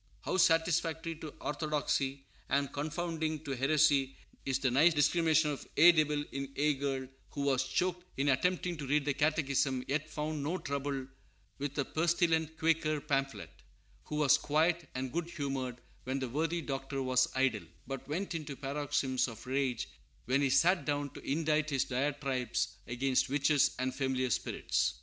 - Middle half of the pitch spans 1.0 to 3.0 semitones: Yes, average, 2.7 semitones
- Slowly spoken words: No, average, 160 wpm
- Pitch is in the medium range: Yes, medium, 145 Hz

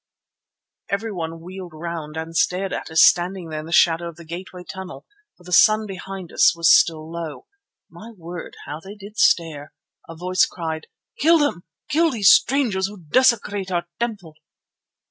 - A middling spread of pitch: Yes, average, 3.4 semitones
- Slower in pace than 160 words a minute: No, average, 165 wpm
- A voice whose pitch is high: No, medium, 180 Hz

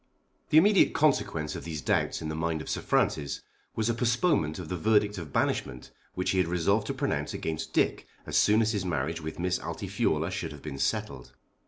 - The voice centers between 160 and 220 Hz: No, very low, 90 Hz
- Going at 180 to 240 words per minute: Yes, fast, 205 wpm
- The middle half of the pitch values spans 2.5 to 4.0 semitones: No, average, 5.3 semitones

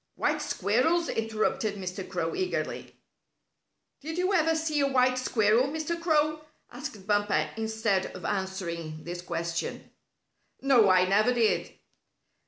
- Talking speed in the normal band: No, slow, 125 wpm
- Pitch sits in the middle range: No, high, 220 Hz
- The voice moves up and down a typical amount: No, wide, 7.9 semitones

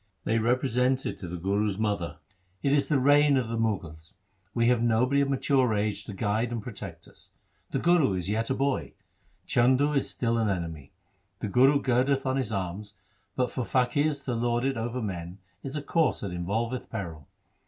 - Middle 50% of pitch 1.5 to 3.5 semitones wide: No, average, 4.6 semitones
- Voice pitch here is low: Yes, low, 115 Hz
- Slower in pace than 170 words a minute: No, average, 190 wpm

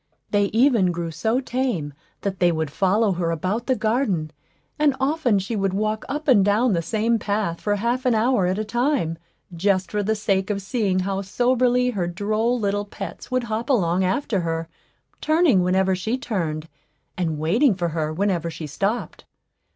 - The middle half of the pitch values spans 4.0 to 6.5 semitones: Yes, average, 4.7 semitones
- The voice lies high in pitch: Yes, high, 205 Hz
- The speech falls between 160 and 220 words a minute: Yes, average, 180 wpm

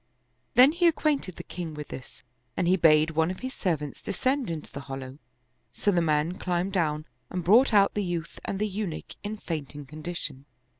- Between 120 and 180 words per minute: No, average, 195 wpm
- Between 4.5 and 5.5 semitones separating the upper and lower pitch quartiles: Yes, average, 5.0 semitones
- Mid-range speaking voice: Yes, medium, 175 Hz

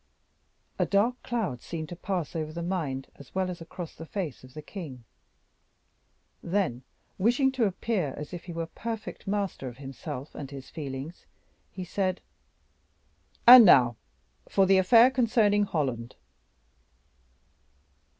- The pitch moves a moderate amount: No, wide, 6.3 semitones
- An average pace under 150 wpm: Yes, average, 140 wpm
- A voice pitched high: No, medium, 175 Hz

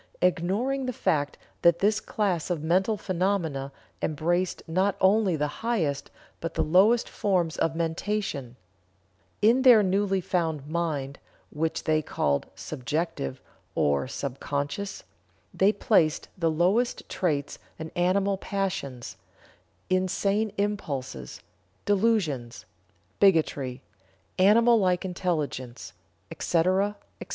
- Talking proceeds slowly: Yes, slow, 110 wpm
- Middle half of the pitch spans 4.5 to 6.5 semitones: Yes, average, 4.9 semitones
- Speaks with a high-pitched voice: No, medium, 175 Hz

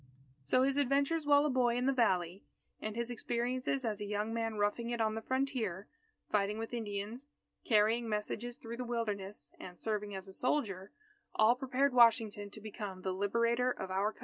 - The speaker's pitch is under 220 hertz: No, high, 225 Hz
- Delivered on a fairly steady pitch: No, average, 3.3 semitones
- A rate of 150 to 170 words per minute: No, average, 185 wpm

